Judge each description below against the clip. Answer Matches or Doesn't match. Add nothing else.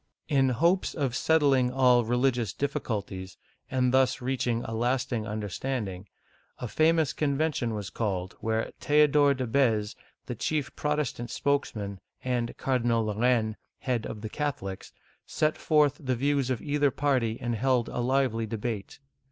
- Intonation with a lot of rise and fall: Doesn't match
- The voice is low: Matches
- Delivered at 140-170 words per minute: Matches